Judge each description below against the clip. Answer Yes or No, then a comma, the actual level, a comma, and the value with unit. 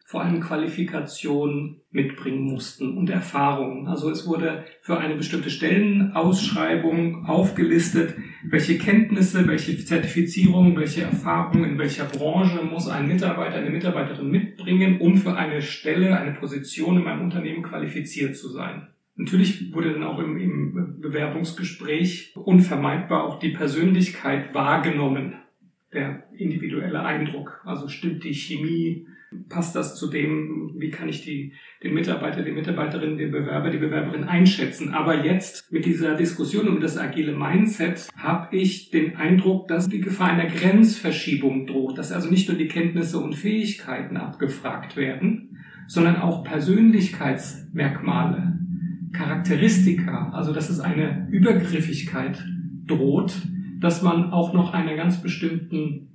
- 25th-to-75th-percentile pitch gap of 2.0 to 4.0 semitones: Yes, average, 2.7 semitones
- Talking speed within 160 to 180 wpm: No, average, 130 wpm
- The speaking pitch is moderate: Yes, medium, 165 Hz